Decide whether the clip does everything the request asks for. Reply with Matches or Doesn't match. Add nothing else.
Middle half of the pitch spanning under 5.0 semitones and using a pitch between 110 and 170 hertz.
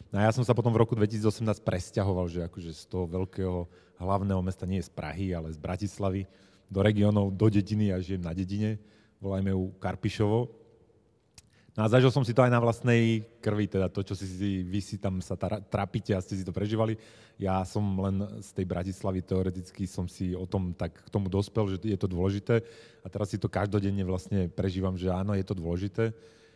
Doesn't match